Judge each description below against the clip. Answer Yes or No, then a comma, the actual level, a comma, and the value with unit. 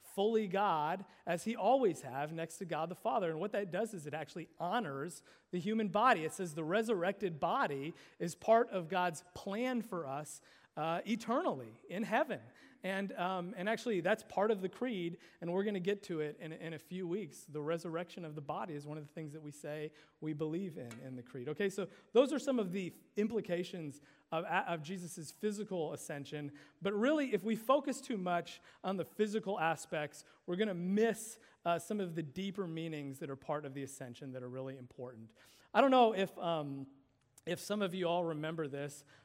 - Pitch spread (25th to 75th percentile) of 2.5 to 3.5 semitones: No, average, 5.0 semitones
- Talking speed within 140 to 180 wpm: No, fast, 205 wpm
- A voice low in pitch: No, medium, 175 Hz